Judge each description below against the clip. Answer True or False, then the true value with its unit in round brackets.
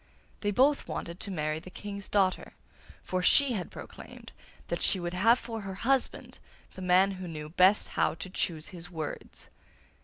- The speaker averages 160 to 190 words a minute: True (175 wpm)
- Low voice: False (185 Hz)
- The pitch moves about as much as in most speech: True (3.1 semitones)